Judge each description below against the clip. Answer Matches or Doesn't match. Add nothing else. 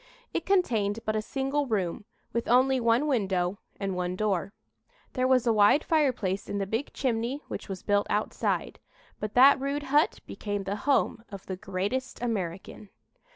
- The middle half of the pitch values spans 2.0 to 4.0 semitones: Doesn't match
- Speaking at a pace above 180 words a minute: Doesn't match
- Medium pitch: Doesn't match